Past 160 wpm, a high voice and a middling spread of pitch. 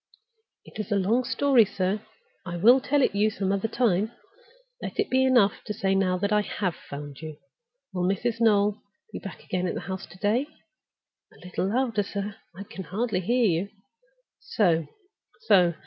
Yes: average, 180 wpm; high, 200 Hz; average, 3.7 semitones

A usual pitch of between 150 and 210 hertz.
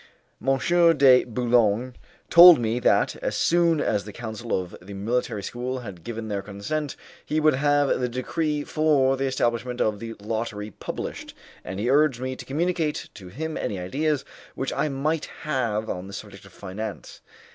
No: low, 125 Hz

